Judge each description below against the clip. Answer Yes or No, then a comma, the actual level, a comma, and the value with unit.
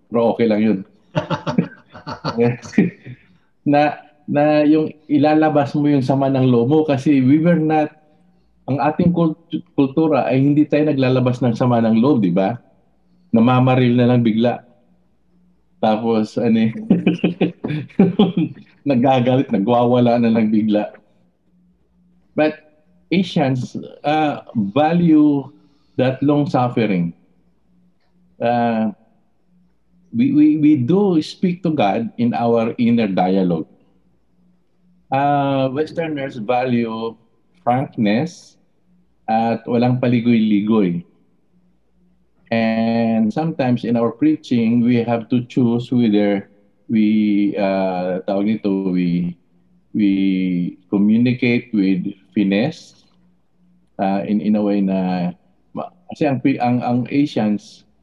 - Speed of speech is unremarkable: No, slow, 100 wpm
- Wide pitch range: Yes, wide, 6.1 semitones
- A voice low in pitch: Yes, low, 125 Hz